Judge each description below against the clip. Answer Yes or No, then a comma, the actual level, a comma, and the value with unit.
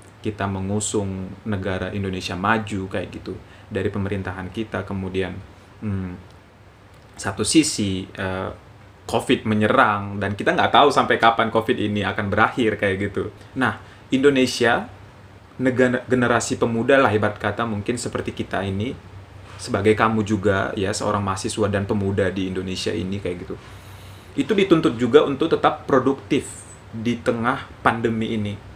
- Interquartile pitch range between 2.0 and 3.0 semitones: Yes, narrow, 2.5 semitones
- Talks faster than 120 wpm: Yes, average, 135 wpm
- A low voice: Yes, low, 105 Hz